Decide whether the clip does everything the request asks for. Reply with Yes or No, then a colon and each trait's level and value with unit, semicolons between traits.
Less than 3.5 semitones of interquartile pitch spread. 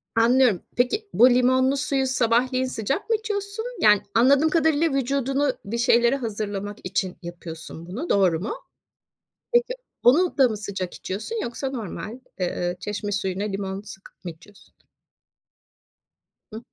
No: average, 5.3 semitones